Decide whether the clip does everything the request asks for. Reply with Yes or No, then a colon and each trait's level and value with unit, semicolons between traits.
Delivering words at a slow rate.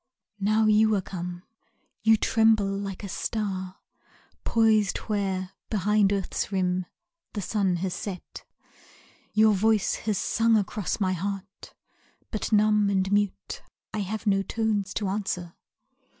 Yes: slow, 130 wpm